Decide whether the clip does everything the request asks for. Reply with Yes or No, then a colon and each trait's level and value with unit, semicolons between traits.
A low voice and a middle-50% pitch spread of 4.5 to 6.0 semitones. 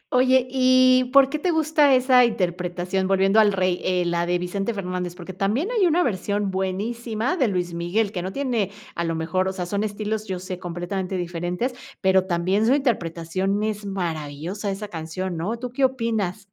No: high, 195 Hz; average, 4.8 semitones